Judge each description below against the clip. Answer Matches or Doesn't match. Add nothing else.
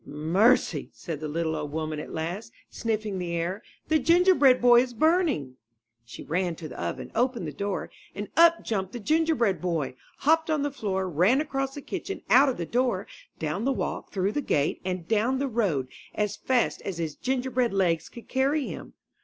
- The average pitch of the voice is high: Matches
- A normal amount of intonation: Doesn't match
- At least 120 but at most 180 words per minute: Doesn't match